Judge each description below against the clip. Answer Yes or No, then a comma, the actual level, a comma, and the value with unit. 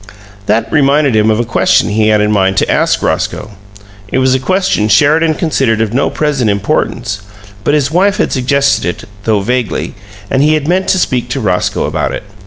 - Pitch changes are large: Yes, wide, 5.7 semitones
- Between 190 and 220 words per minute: Yes, average, 195 wpm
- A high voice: No, low, 130 Hz